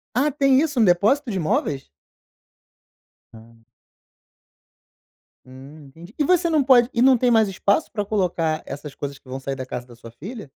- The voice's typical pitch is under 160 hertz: No, high, 190 Hz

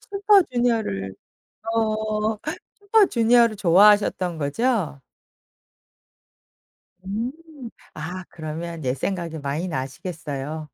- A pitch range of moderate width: No, wide, 6.6 semitones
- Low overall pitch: No, medium, 185 Hz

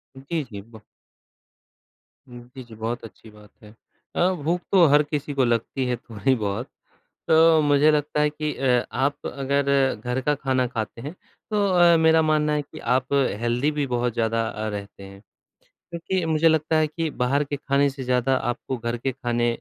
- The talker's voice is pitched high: No, low, 135 Hz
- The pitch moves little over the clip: No, average, 4.1 semitones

